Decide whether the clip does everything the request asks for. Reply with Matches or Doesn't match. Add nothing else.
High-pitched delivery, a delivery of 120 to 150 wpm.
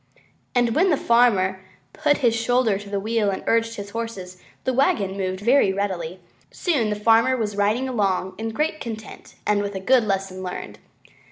Doesn't match